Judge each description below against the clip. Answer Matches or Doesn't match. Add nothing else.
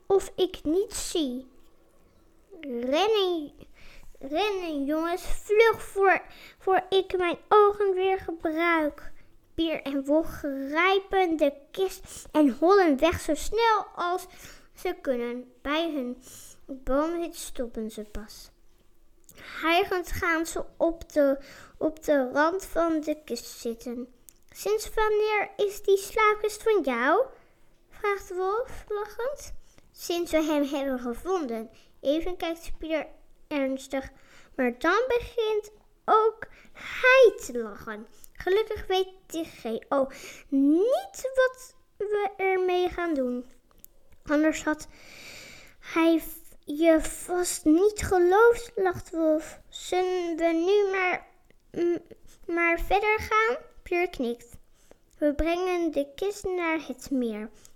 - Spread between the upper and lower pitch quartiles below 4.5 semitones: Doesn't match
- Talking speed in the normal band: Doesn't match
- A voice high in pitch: Matches